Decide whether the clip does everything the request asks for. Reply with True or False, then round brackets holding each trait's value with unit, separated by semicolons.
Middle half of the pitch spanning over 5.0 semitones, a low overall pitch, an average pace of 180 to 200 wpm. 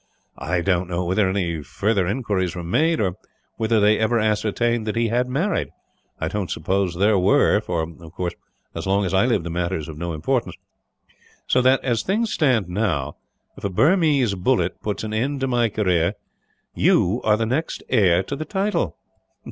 True (5.4 semitones; 105 Hz; 190 wpm)